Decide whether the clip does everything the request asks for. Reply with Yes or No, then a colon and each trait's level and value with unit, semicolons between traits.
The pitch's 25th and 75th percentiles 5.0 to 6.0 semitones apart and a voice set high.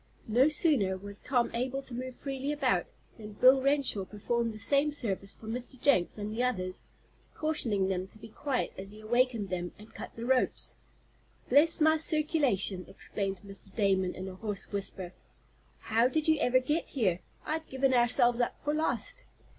Yes: wide, 5.5 semitones; high, 240 Hz